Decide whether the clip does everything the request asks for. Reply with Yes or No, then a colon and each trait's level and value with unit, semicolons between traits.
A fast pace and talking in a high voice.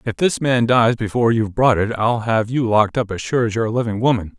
No: fast, 275 wpm; low, 115 Hz